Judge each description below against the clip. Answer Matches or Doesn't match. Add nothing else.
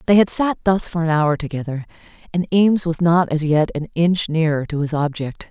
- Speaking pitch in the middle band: Matches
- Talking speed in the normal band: Doesn't match